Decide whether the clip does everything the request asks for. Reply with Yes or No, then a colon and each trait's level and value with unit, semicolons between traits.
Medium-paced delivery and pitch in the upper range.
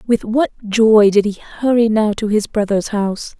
Yes: average, 195 wpm; high, 215 Hz